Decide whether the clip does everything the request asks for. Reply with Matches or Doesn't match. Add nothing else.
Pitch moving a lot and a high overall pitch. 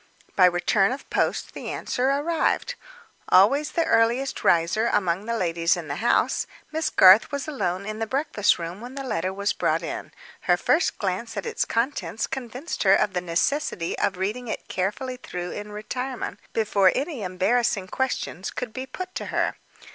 Matches